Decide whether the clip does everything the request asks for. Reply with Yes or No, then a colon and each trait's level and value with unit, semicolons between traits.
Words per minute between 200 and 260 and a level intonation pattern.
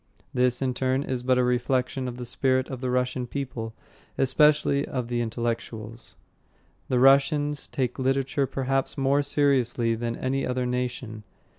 No: average, 150 wpm; narrow, 1.8 semitones